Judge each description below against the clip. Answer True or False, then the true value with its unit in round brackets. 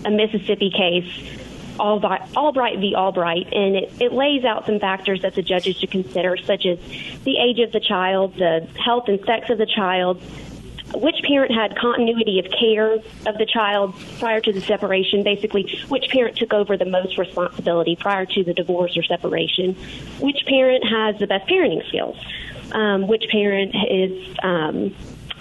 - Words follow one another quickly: False (170 wpm)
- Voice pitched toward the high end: True (205 Hz)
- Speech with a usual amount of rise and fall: True (3.0 semitones)